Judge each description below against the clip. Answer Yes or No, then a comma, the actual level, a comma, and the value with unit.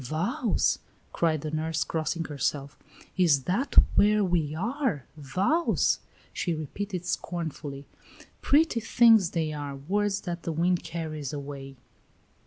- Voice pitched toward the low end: No, medium, 165 Hz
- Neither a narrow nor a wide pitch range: Yes, average, 5.0 semitones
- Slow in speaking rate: Yes, slow, 120 wpm